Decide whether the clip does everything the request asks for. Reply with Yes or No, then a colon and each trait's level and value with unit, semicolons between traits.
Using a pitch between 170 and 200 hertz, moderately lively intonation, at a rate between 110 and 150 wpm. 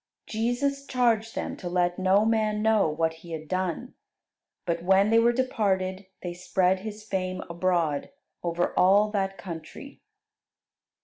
Yes: high, 190 Hz; average, 3.7 semitones; average, 140 wpm